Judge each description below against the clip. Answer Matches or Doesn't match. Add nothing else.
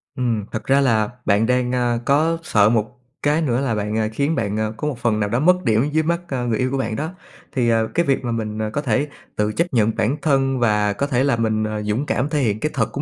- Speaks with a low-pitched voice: Matches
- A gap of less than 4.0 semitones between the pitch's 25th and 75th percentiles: Doesn't match